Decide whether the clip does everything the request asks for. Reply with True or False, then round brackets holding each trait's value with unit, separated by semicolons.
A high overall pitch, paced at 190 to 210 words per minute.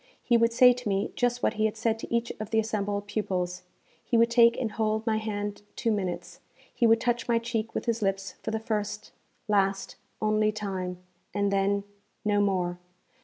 True (215 Hz; 195 wpm)